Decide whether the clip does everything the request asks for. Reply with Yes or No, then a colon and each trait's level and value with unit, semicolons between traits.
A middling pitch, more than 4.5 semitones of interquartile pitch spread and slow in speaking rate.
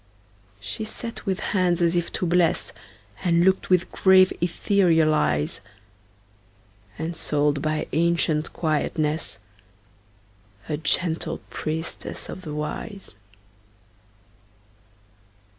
No: medium, 165 Hz; average, 2.9 semitones; slow, 90 wpm